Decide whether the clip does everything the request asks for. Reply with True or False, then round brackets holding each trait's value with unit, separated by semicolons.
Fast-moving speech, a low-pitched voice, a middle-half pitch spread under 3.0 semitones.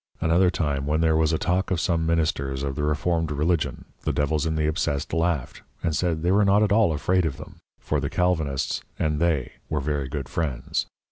True (210 wpm; 80 Hz; 2.6 semitones)